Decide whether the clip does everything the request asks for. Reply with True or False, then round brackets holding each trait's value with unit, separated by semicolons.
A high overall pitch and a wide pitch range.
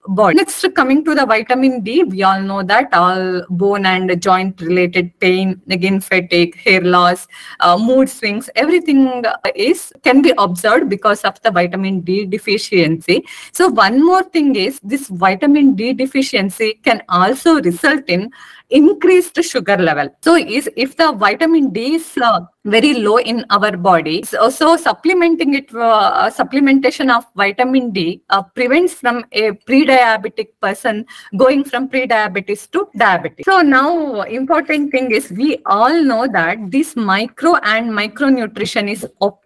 True (230 Hz; 6.0 semitones)